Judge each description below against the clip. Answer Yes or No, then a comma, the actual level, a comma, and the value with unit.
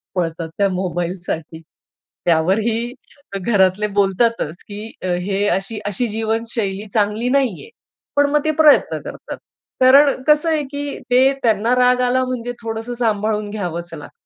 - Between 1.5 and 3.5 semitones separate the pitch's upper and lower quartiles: No, average, 4.6 semitones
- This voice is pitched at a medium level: No, high, 220 Hz